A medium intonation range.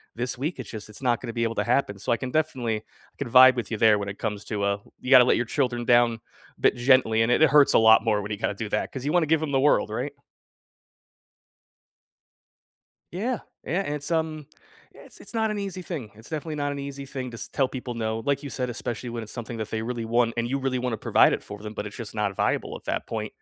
Yes: average, 4.1 semitones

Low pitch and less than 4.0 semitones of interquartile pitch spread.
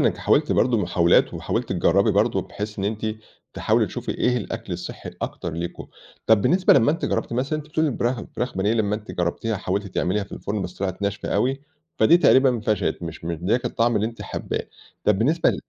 No: low, 110 Hz; average, 4.3 semitones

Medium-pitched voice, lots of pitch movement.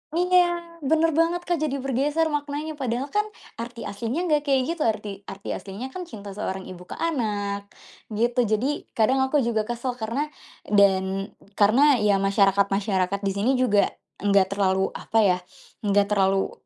No: high, 230 Hz; wide, 6.6 semitones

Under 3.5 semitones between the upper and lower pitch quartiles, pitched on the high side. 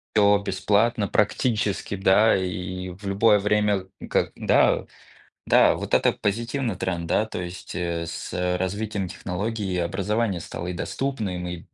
No: average, 2.8 semitones; low, 100 Hz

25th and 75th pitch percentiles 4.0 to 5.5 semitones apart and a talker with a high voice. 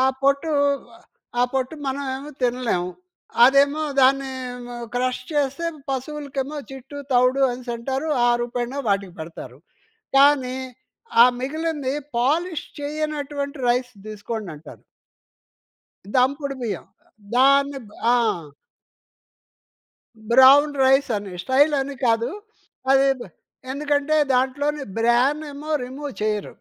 No: average, 2.7 semitones; very high, 270 Hz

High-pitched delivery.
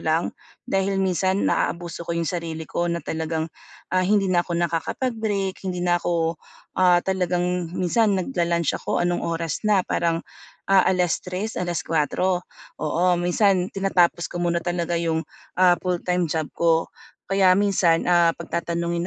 No: medium, 175 Hz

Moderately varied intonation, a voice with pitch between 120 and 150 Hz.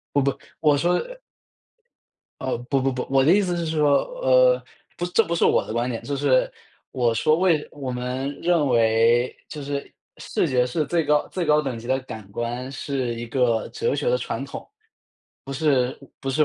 Yes: average, 4.4 semitones; medium, 140 Hz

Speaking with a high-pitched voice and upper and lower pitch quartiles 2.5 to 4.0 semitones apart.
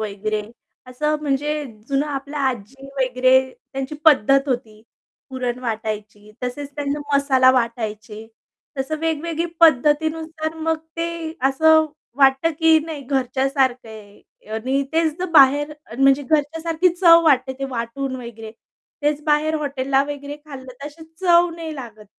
Yes: very high, 275 Hz; average, 3.4 semitones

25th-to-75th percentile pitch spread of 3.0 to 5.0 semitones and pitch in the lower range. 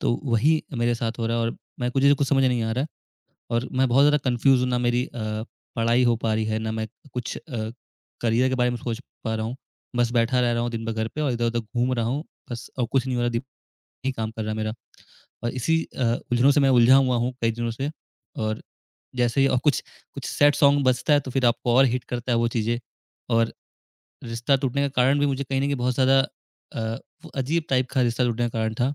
No: narrow, 2.6 semitones; low, 120 Hz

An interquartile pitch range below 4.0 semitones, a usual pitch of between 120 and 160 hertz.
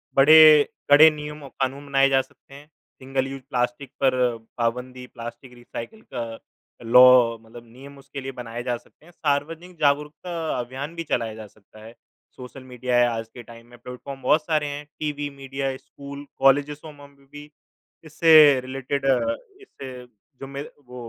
Yes: average, 2.8 semitones; low, 135 Hz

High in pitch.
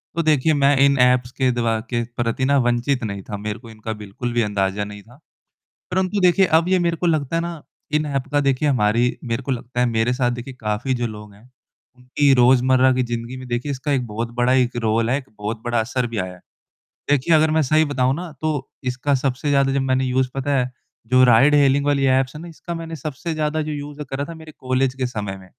No: low, 130 Hz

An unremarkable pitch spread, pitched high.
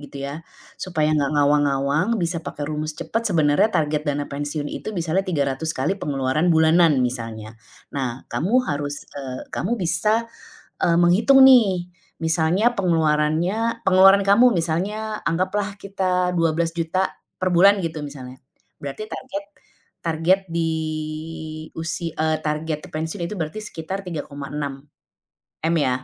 No: average, 3.6 semitones; medium, 160 Hz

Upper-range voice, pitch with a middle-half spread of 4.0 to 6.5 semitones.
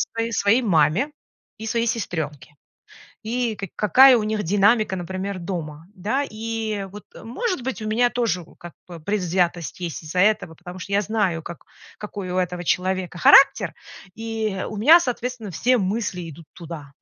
Yes: high, 200 Hz; average, 4.4 semitones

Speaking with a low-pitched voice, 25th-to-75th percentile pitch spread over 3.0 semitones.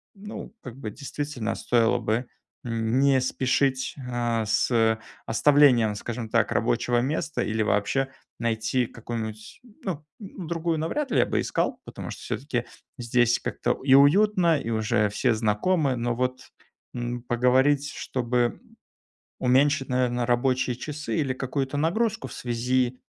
Yes: low, 125 Hz; average, 3.5 semitones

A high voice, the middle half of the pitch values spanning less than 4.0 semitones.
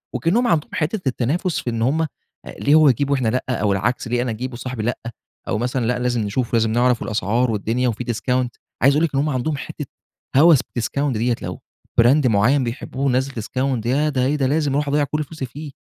No: low, 130 Hz; average, 3.3 semitones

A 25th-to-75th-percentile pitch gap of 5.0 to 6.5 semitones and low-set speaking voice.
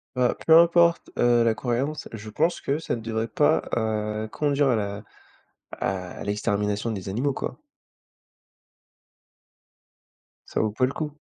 Yes: average, 5.3 semitones; low, 115 Hz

